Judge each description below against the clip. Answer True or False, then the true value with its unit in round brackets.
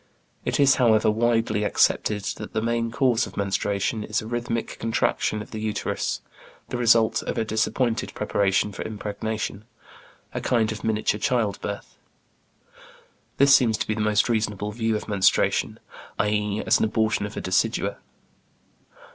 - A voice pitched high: False (110 Hz)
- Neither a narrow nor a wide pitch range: False (1.7 semitones)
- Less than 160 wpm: True (150 wpm)